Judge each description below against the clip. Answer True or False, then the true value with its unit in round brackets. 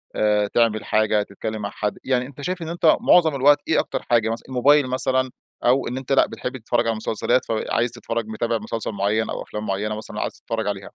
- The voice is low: True (115 Hz)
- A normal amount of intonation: True (3.3 semitones)